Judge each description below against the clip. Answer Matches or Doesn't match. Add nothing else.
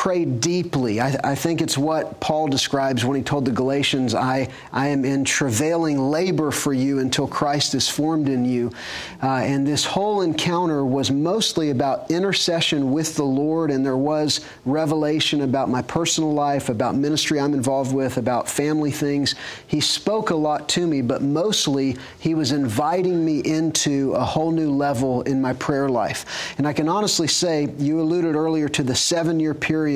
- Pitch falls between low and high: Matches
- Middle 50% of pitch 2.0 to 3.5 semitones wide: Matches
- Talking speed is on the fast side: Doesn't match